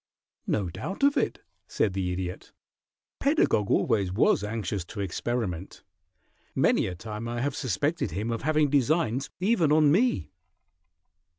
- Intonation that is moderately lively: No, wide, 7.9 semitones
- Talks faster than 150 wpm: No, slow, 135 wpm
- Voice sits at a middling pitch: No, low, 115 Hz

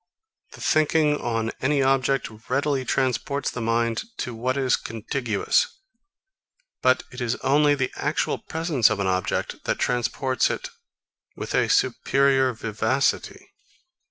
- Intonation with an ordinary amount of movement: Yes, average, 3.2 semitones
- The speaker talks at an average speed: No, slow, 130 wpm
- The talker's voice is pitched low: Yes, low, 130 Hz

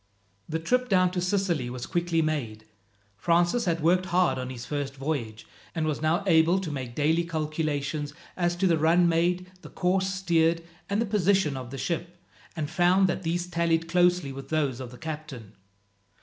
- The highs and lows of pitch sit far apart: No, average, 3.5 semitones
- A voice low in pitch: No, medium, 165 Hz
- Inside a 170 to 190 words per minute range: Yes, average, 180 wpm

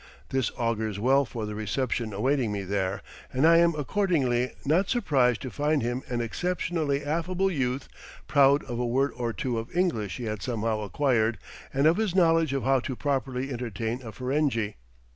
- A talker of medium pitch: No, low, 130 Hz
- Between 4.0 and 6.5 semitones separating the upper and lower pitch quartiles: Yes, average, 4.4 semitones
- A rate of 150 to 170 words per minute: No, average, 180 wpm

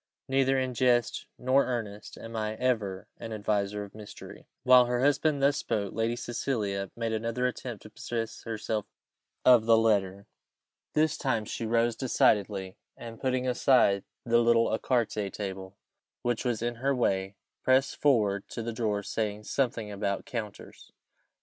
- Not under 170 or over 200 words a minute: No, average, 150 wpm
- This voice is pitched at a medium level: No, low, 115 Hz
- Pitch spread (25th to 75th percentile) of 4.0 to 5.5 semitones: No, average, 3.3 semitones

